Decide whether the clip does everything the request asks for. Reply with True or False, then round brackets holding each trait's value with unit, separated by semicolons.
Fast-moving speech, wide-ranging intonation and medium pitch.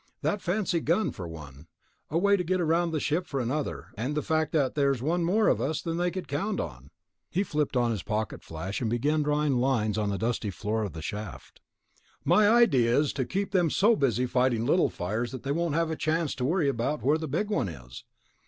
True (220 wpm; 6.6 semitones; 145 Hz)